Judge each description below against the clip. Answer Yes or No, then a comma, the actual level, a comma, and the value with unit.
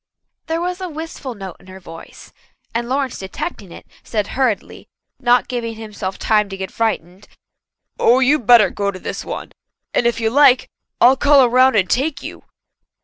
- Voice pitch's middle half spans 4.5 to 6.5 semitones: Yes, average, 4.8 semitones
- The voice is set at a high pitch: Yes, high, 235 Hz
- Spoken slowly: No, average, 175 wpm